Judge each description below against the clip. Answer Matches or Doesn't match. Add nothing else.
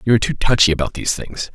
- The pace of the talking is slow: Doesn't match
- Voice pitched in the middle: Doesn't match